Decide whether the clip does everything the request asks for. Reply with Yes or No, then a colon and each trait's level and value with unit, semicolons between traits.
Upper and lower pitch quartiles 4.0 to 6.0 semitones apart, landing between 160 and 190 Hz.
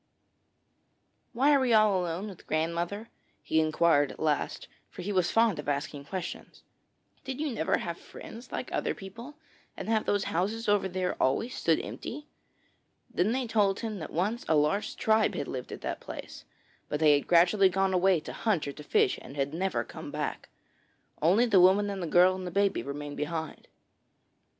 Yes: average, 5.1 semitones; medium, 185 Hz